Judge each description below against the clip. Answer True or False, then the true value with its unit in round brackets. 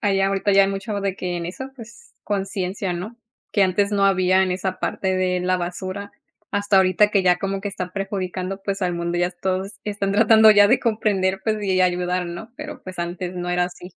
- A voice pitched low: False (190 Hz)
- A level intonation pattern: True (1.9 semitones)